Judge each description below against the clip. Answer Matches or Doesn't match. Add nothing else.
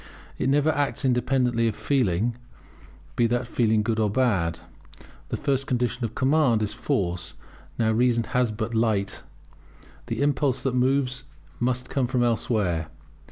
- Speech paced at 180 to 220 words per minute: Doesn't match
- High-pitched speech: Doesn't match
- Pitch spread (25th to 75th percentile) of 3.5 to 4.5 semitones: Doesn't match